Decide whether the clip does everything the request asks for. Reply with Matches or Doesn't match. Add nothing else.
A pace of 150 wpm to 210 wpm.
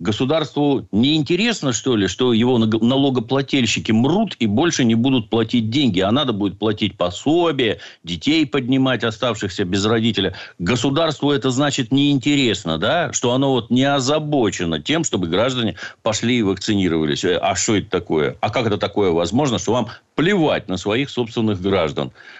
Matches